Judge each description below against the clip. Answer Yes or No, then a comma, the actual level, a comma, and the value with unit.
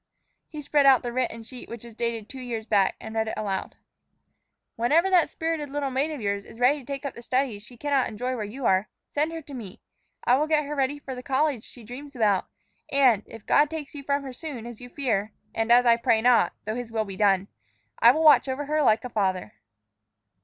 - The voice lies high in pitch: Yes, very high, 250 Hz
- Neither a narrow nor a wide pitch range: Yes, average, 4.3 semitones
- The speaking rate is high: Yes, fast, 235 wpm